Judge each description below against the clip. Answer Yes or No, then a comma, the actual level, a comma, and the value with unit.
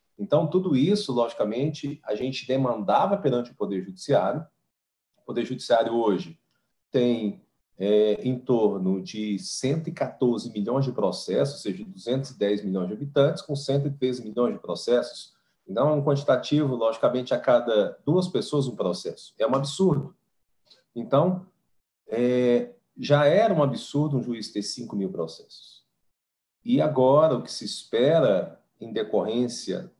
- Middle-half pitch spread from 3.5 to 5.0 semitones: Yes, average, 4.3 semitones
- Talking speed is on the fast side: No, average, 140 wpm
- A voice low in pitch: Yes, low, 130 Hz